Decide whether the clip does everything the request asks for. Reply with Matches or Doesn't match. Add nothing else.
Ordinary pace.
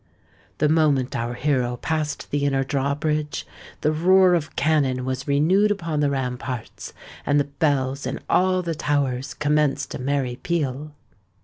Matches